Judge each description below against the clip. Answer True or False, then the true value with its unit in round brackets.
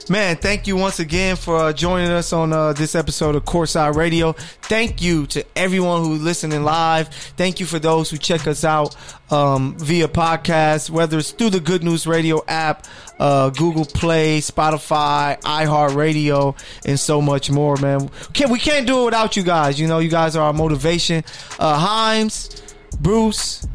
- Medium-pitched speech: True (160 Hz)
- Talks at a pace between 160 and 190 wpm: True (175 wpm)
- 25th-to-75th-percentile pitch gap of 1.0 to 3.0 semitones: True (2.4 semitones)